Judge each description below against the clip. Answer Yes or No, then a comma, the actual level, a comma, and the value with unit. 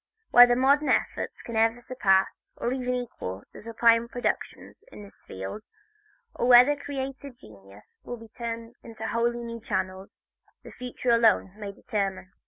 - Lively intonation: No, average, 3.3 semitones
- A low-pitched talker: No, high, 230 Hz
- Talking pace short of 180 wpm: Yes, average, 150 wpm